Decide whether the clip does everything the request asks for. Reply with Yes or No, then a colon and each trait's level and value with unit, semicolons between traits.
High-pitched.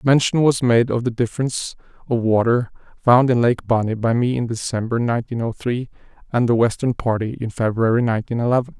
No: low, 120 Hz